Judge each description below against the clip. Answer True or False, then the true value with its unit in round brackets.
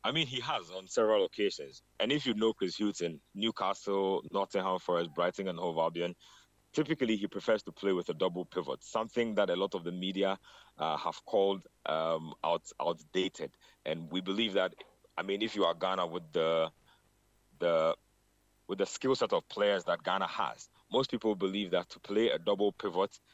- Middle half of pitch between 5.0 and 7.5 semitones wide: True (5.3 semitones)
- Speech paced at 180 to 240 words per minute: True (190 wpm)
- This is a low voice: True (100 Hz)